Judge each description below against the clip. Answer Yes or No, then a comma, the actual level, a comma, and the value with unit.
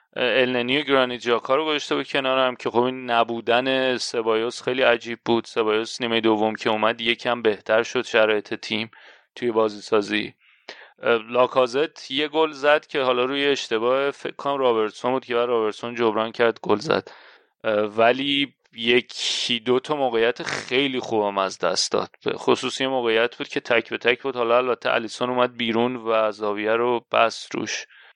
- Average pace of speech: No, fast, 165 wpm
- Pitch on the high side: No, low, 120 Hz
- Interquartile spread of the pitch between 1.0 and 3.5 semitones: Yes, narrow, 2.5 semitones